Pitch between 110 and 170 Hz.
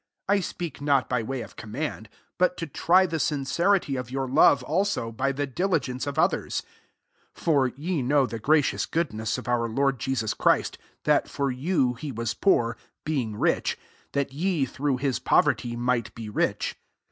Yes: low, 135 Hz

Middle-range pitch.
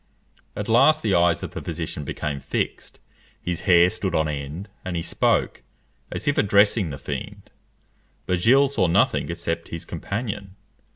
No: very low, 90 Hz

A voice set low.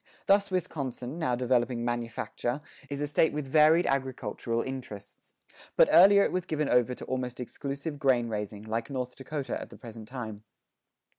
Yes: low, 130 Hz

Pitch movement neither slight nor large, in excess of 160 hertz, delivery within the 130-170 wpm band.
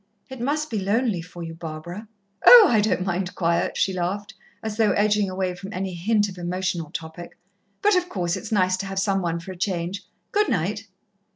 No: average, 3.4 semitones; high, 190 Hz; average, 200 wpm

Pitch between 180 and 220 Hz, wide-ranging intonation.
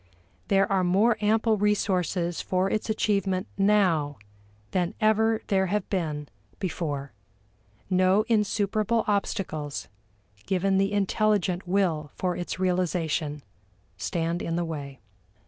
No: medium, 185 Hz; average, 3.4 semitones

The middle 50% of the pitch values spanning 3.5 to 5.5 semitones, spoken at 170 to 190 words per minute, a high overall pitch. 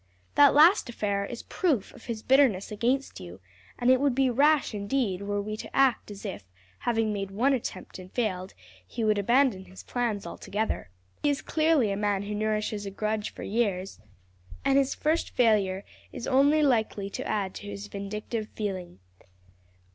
Yes: average, 4.5 semitones; average, 175 wpm; high, 215 Hz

